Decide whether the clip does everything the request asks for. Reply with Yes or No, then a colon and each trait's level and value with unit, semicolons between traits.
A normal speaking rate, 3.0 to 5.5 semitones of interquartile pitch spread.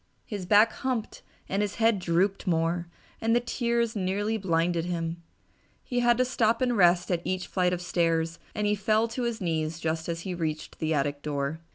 Yes: average, 195 wpm; average, 5.0 semitones